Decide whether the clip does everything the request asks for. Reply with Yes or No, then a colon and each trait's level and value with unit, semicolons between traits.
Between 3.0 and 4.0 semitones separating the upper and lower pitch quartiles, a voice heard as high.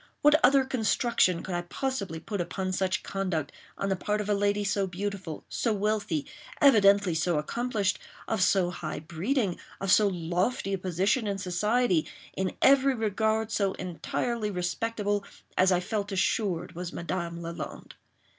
Yes: average, 3.4 semitones; high, 195 Hz